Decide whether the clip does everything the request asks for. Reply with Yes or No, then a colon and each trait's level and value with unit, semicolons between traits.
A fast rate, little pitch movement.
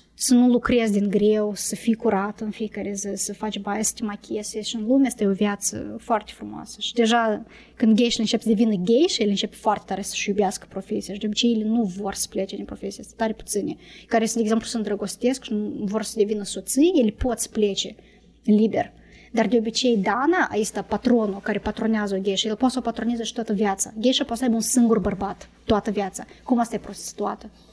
Yes: fast, 220 wpm; narrow, 2.2 semitones